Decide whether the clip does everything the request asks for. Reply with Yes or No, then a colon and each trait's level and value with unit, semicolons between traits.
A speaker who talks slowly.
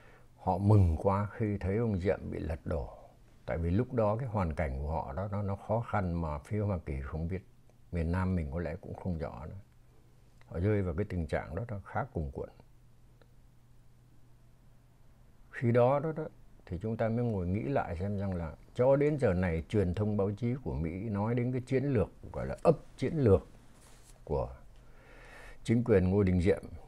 No: average, 200 wpm